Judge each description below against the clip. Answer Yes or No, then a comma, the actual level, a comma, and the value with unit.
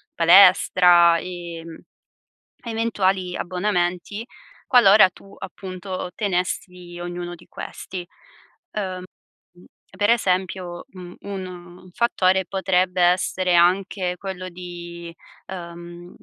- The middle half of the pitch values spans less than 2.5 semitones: Yes, narrow, 1.5 semitones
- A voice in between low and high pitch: Yes, medium, 180 Hz